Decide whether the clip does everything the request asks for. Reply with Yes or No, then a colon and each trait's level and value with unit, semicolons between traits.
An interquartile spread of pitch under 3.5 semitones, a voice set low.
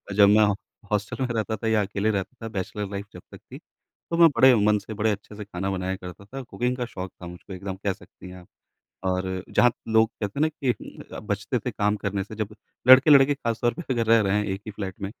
Yes: average, 2.8 semitones; low, 105 Hz